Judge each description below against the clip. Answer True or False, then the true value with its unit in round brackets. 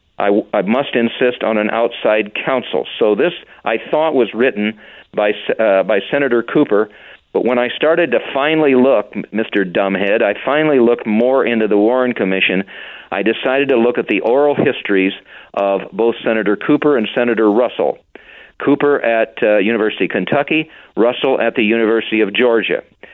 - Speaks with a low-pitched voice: True (115 Hz)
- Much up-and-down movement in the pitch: False (3.3 semitones)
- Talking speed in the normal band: True (165 wpm)